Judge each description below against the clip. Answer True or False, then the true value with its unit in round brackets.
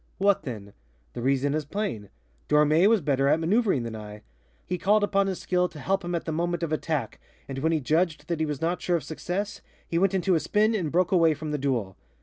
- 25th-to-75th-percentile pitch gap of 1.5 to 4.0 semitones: False (4.6 semitones)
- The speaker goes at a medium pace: False (235 wpm)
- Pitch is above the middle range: False (165 Hz)